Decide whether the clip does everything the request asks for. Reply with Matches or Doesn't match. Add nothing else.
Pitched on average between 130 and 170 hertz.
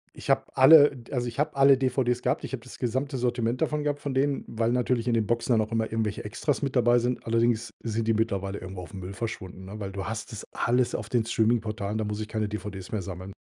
Doesn't match